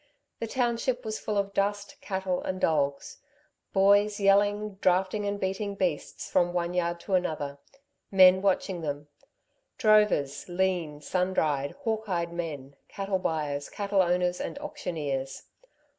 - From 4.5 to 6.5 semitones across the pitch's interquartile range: No, average, 3.6 semitones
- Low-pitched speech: No, medium, 185 Hz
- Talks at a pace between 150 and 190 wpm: No, slow, 135 wpm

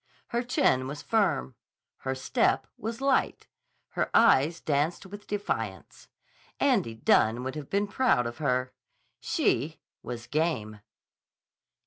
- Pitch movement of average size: No, wide, 8.4 semitones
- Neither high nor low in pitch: Yes, medium, 145 Hz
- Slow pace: Yes, slow, 120 wpm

